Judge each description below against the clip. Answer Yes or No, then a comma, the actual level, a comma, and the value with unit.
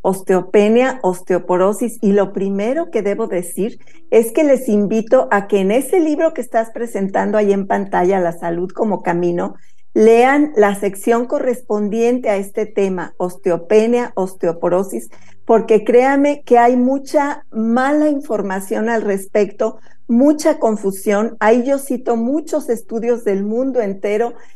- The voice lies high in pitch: Yes, high, 220 Hz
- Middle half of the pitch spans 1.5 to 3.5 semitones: No, average, 3.9 semitones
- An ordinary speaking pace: Yes, average, 135 wpm